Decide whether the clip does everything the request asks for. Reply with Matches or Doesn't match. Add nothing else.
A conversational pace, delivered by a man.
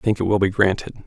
Doesn't match